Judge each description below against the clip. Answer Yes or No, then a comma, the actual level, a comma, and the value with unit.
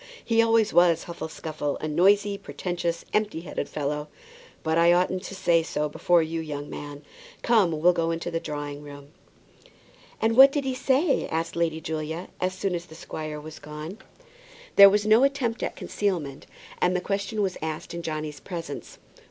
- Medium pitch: Yes, medium, 170 Hz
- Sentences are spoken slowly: No, average, 175 wpm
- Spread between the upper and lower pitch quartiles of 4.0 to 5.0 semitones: Yes, average, 4.4 semitones